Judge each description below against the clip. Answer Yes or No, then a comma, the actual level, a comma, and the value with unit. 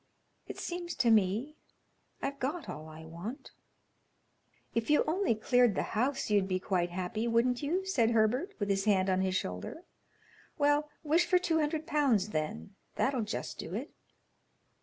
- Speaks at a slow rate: No, average, 165 wpm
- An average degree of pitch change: No, wide, 7.3 semitones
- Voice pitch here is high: Yes, high, 230 Hz